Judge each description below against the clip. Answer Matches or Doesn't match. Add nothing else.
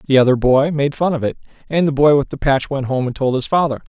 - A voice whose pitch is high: Doesn't match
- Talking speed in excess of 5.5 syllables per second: Matches